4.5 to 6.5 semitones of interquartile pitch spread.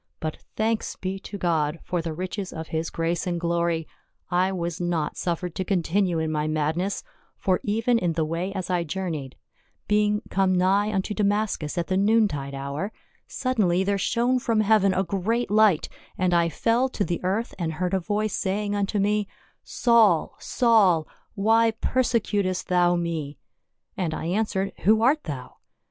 No: average, 3.7 semitones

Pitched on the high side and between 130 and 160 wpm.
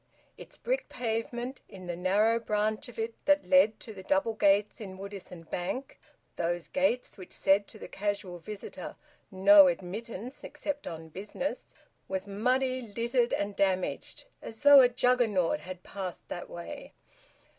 Yes: high, 210 Hz; average, 150 wpm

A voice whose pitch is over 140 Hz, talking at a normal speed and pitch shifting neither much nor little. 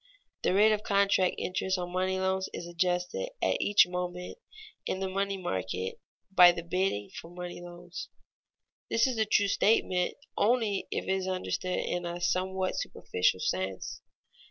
No: medium, 185 Hz; average, 155 wpm; narrow, 1.8 semitones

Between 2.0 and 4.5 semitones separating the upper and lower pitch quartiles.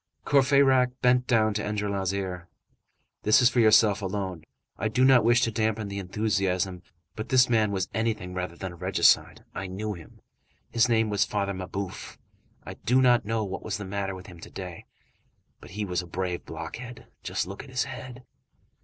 Yes: average, 3.8 semitones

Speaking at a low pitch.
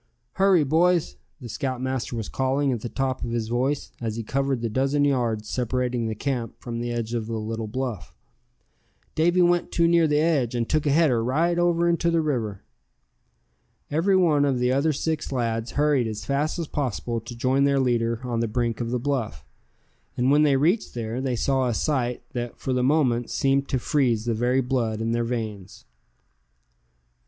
Yes: low, 130 Hz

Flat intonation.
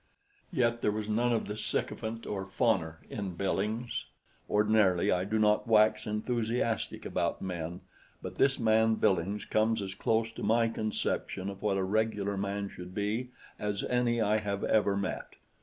Yes: narrow, 2.3 semitones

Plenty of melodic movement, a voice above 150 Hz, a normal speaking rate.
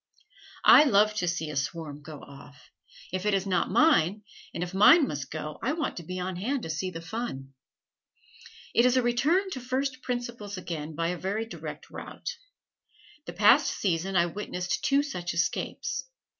Yes: wide, 6.8 semitones; high, 190 Hz; average, 180 wpm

